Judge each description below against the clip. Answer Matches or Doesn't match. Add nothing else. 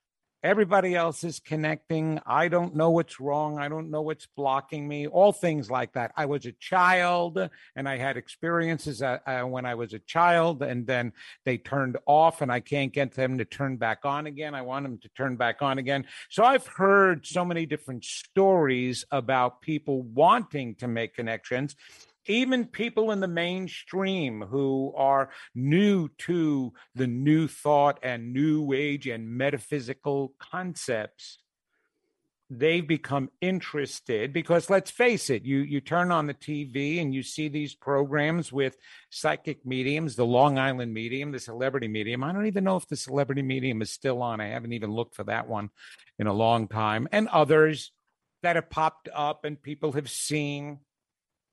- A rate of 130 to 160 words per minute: Doesn't match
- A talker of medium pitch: Matches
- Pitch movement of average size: Matches